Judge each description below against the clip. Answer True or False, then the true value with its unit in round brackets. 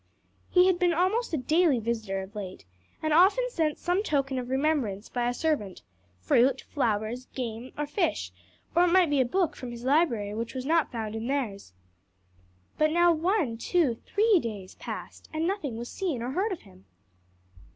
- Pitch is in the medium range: False (270 Hz)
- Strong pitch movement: True (6.9 semitones)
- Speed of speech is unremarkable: True (180 wpm)